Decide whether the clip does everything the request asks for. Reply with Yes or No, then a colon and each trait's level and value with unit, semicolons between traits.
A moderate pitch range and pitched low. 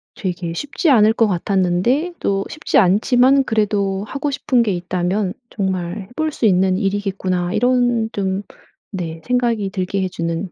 No: average, 4.5 semitones; high, 200 Hz